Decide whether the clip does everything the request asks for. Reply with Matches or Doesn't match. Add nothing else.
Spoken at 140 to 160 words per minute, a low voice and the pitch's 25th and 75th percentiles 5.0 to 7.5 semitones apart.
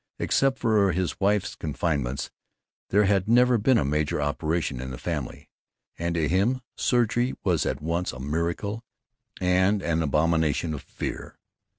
Matches